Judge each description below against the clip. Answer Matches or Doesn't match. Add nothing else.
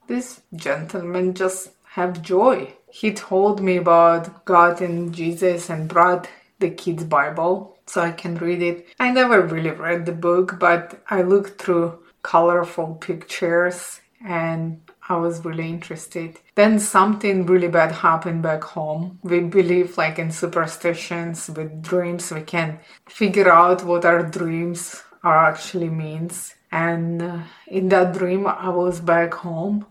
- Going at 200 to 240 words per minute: Doesn't match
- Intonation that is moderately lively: Doesn't match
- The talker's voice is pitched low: Doesn't match